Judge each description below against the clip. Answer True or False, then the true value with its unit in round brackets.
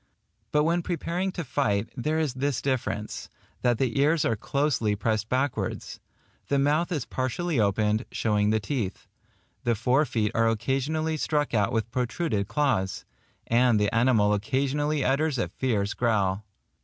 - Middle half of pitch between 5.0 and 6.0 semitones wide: True (5.3 semitones)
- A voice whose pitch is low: True (125 Hz)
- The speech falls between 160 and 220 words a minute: False (150 wpm)